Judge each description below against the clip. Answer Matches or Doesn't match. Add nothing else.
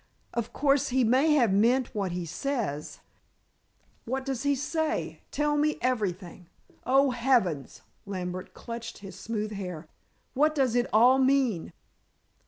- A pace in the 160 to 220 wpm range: Doesn't match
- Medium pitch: Doesn't match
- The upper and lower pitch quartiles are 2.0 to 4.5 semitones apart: Doesn't match